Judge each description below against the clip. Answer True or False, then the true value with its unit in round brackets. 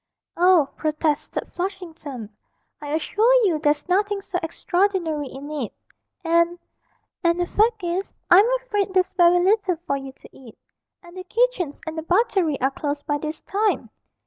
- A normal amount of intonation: True (4.4 semitones)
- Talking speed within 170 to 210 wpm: False (155 wpm)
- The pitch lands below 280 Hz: False (345 Hz)